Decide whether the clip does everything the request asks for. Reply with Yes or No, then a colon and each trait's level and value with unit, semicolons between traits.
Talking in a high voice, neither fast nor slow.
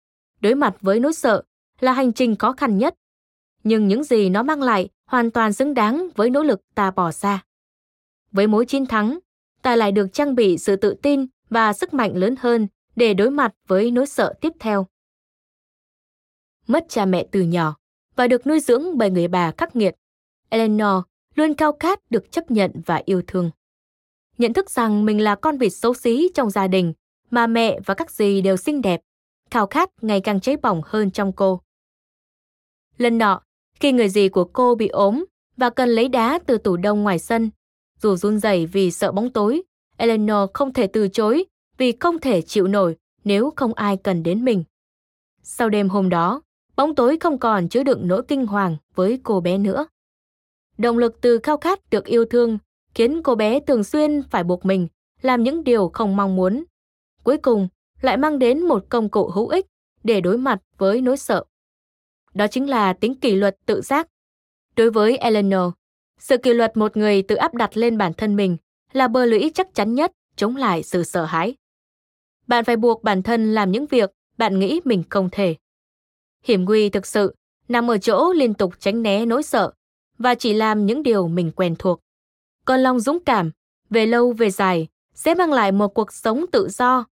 Yes: high, 225 Hz; average, 195 wpm